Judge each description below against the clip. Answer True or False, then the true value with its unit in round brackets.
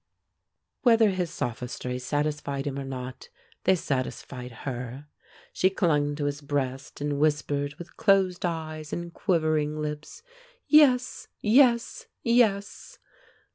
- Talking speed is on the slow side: True (115 wpm)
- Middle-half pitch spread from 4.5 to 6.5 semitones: True (5.1 semitones)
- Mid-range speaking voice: True (150 Hz)